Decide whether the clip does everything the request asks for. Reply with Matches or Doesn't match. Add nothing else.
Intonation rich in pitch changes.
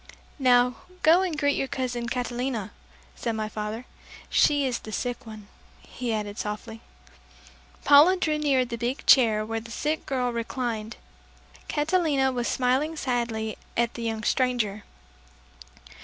Doesn't match